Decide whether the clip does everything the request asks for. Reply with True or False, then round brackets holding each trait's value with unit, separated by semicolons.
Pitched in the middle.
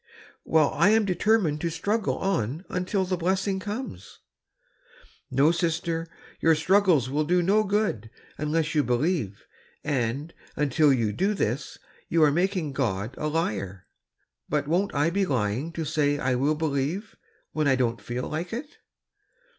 True (155 Hz)